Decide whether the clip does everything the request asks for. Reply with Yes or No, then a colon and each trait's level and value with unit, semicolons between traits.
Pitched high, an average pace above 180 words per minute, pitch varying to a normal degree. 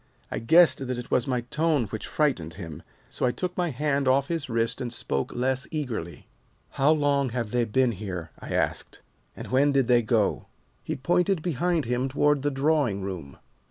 No: low, 130 Hz; average, 190 wpm; average, 4.3 semitones